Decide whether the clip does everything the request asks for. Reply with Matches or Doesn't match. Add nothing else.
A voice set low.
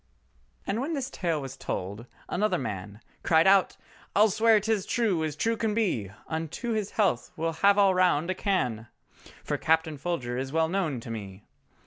Doesn't match